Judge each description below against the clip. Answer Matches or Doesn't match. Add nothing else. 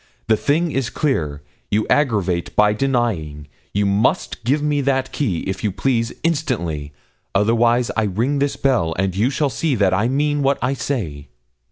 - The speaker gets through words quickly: Doesn't match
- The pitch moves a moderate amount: Doesn't match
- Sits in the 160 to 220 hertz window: Doesn't match